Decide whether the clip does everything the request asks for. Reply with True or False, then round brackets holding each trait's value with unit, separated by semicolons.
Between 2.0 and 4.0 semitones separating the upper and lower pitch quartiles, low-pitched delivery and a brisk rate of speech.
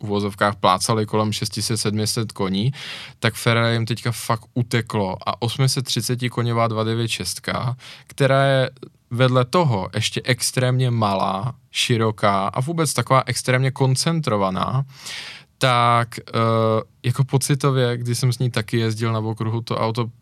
False (2.5 semitones; 120 Hz; 125 wpm)